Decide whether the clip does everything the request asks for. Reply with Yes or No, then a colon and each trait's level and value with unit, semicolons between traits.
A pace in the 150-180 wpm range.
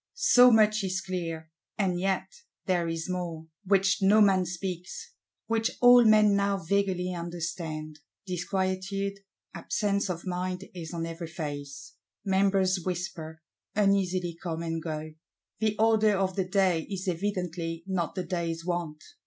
No: slow, 135 wpm